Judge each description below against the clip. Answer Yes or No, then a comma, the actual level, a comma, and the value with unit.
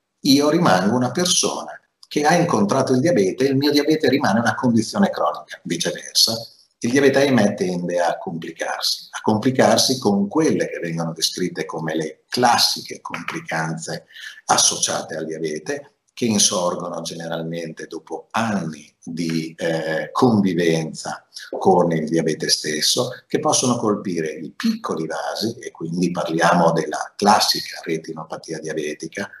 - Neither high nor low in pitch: No, very low, 85 Hz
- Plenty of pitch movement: Yes, wide, 7.6 semitones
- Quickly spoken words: No, average, 130 wpm